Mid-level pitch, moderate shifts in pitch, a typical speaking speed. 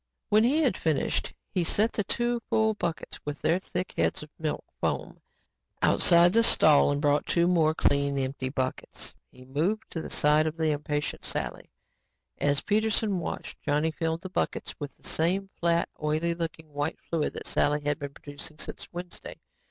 Yes: medium, 160 Hz; average, 3.6 semitones; average, 175 wpm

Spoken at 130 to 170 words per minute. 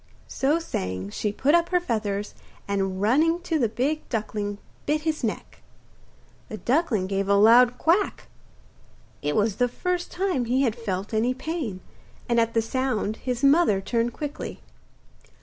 Yes: average, 155 wpm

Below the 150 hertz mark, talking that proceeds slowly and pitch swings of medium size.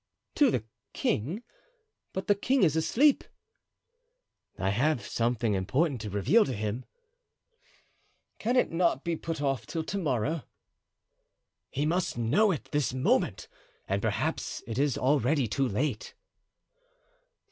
No: medium, 140 Hz; slow, 130 wpm; wide, 6.4 semitones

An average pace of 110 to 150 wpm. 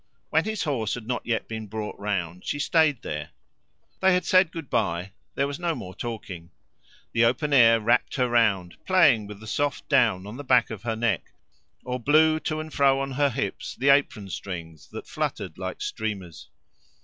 No: average, 190 wpm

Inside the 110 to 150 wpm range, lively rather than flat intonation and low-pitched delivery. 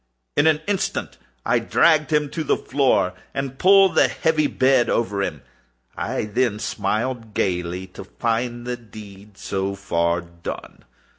Yes: average, 145 wpm; wide, 6.0 semitones; low, 115 Hz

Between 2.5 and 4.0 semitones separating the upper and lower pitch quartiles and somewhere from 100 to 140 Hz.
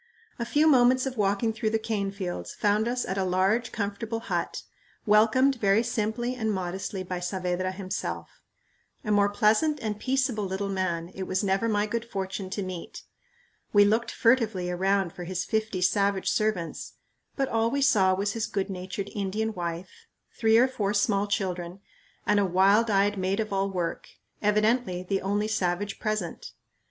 No: average, 2.9 semitones; high, 205 Hz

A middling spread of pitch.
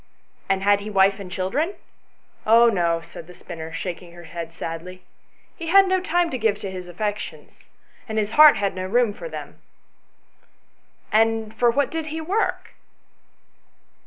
No: wide, 5.8 semitones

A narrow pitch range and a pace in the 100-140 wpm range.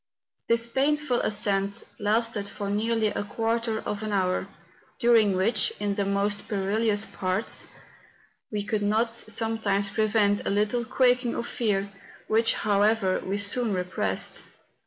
Yes: narrow, 2.2 semitones; slow, 135 wpm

